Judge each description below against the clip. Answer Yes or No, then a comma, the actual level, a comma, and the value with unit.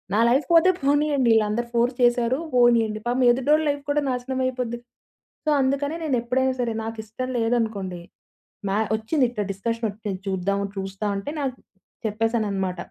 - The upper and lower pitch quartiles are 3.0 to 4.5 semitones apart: Yes, average, 3.5 semitones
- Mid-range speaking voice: No, high, 240 Hz